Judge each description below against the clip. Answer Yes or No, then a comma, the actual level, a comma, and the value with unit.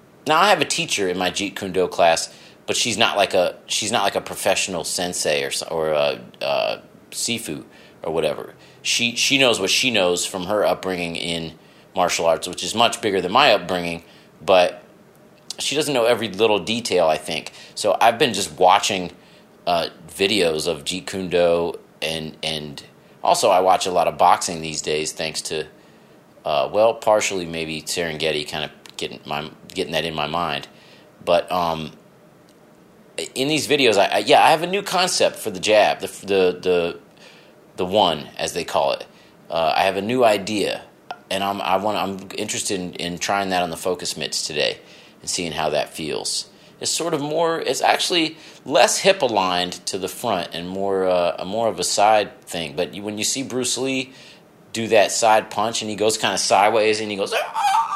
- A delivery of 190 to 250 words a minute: Yes, average, 195 wpm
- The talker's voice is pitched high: No, very low, 95 Hz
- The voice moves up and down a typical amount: No, wide, 5.9 semitones